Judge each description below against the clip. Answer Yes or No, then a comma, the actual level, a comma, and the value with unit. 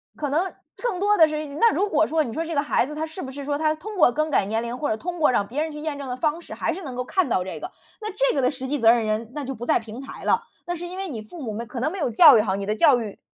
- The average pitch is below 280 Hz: No, very high, 290 Hz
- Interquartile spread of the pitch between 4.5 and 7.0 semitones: Yes, wide, 5.5 semitones